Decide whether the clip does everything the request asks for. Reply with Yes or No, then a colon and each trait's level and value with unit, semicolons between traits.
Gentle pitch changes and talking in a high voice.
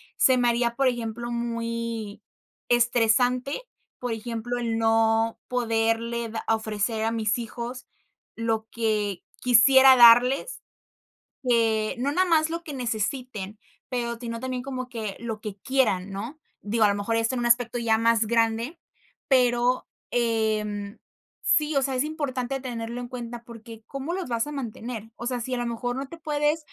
Yes: narrow, 2.1 semitones; high, 235 Hz